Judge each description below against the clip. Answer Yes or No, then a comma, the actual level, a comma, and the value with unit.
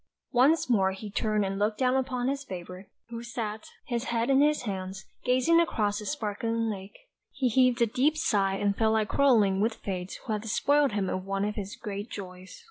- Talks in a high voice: Yes, high, 220 Hz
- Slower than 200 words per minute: No, fast, 205 wpm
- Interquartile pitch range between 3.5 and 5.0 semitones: Yes, average, 4.2 semitones